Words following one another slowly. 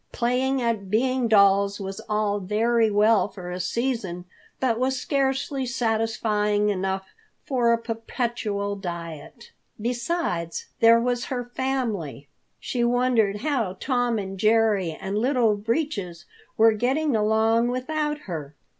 Yes: slow, 125 wpm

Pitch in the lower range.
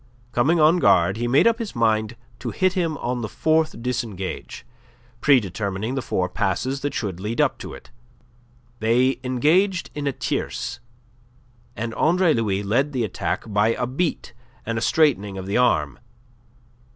Yes: low, 120 Hz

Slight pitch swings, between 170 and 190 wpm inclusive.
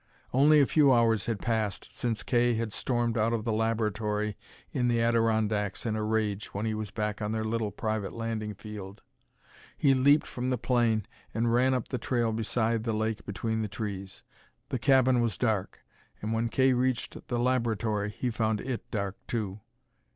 Yes: narrow, 2.1 semitones; average, 180 wpm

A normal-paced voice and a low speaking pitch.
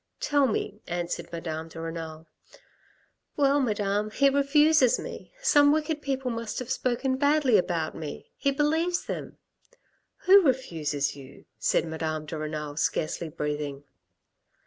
No: average, 145 wpm; high, 210 Hz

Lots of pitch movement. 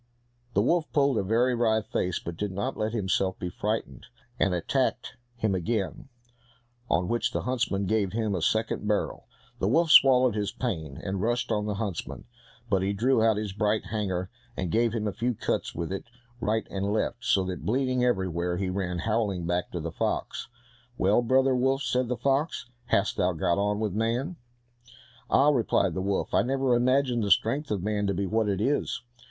No: average, 4.3 semitones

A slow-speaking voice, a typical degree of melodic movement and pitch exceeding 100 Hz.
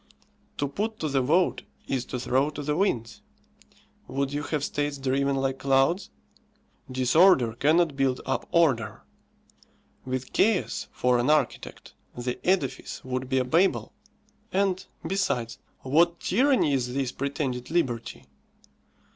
Yes: slow, 130 wpm; average, 4.4 semitones; medium, 140 Hz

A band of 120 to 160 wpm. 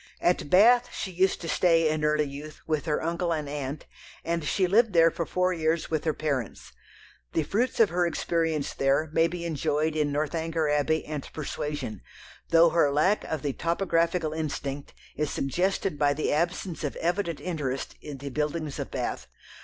No: average, 175 wpm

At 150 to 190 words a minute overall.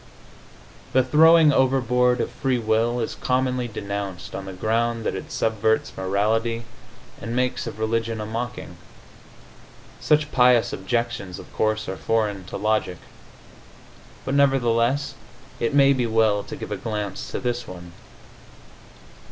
No: slow, 135 wpm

